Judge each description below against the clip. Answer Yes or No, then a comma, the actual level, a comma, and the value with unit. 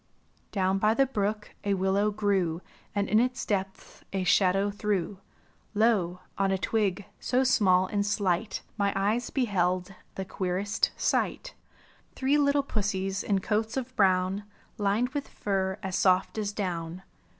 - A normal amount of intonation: No, narrow, 2.3 semitones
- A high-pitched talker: Yes, high, 200 Hz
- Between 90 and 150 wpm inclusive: Yes, average, 145 wpm